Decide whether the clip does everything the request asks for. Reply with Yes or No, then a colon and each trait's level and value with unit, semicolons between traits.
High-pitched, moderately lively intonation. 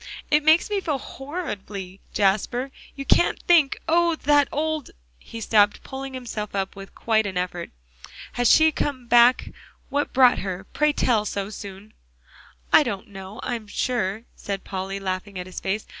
No: high, 225 Hz; wide, 6.2 semitones